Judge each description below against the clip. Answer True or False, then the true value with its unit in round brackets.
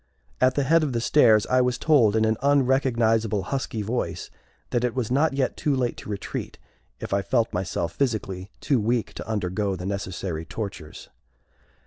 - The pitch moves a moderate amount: True (4.7 semitones)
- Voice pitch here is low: True (115 Hz)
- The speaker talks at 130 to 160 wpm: False (175 wpm)